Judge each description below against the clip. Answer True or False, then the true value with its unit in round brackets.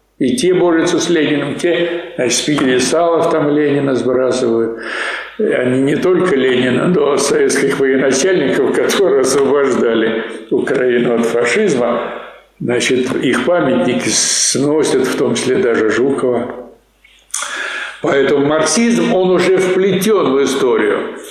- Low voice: False (150 Hz)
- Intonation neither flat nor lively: False (6.3 semitones)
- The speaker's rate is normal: True (120 wpm)